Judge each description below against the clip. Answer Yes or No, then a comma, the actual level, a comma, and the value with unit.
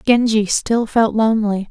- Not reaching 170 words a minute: Yes, average, 140 wpm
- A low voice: No, high, 220 Hz